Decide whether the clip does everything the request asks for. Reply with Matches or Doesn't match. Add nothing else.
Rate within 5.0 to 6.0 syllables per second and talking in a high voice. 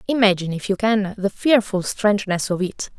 Matches